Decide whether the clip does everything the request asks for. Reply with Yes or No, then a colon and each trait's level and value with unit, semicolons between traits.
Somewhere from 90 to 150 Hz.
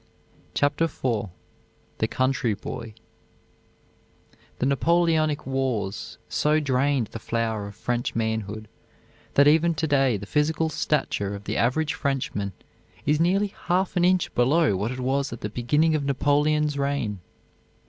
Yes: medium, 140 Hz